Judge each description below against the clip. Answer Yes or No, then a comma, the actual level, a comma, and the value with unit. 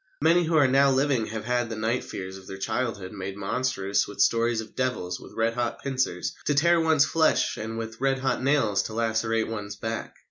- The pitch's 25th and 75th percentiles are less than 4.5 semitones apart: Yes, average, 3.8 semitones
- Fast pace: Yes, fast, 210 wpm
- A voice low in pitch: Yes, low, 115 Hz